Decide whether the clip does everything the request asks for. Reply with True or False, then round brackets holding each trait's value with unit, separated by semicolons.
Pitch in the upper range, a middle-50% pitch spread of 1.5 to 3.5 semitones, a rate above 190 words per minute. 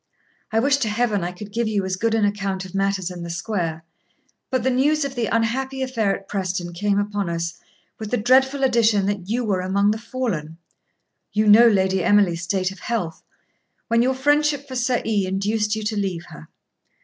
False (210 Hz; 4.0 semitones; 200 wpm)